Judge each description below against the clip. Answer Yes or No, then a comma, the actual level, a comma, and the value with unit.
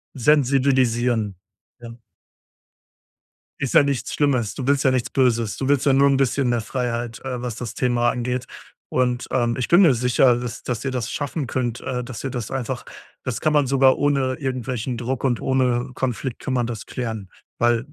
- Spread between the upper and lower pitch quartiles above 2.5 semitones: No, narrow, 2.0 semitones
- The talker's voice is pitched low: Yes, low, 125 Hz